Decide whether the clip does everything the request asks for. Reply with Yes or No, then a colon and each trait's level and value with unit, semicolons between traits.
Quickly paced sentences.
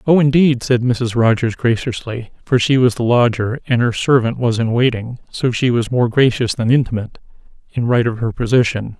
No: average, 195 wpm